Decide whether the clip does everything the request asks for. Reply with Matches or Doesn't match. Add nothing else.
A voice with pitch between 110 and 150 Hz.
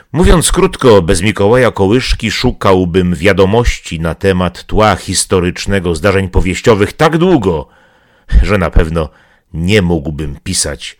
Doesn't match